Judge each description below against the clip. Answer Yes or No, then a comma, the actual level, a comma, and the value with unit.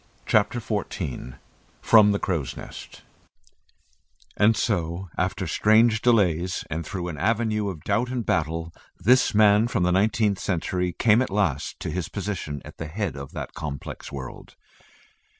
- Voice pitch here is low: Yes, very low, 95 Hz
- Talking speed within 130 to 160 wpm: Yes, average, 150 wpm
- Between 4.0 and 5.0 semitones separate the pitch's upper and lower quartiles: Yes, average, 4.7 semitones